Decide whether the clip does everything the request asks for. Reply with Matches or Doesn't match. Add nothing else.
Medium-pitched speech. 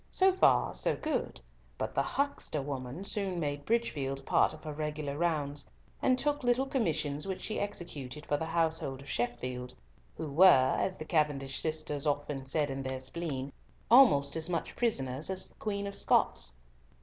Matches